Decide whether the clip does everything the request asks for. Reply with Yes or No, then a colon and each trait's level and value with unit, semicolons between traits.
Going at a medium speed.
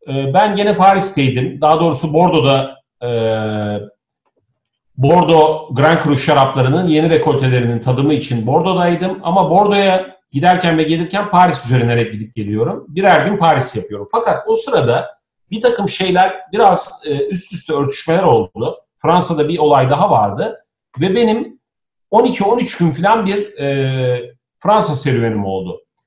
Yes: average, 120 wpm